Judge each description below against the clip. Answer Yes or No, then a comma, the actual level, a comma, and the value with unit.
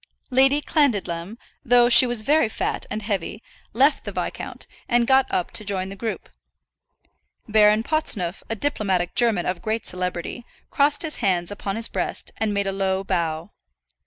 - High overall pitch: Yes, high, 215 Hz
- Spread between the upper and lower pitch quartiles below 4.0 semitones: No, average, 4.3 semitones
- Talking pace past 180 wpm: No, average, 160 wpm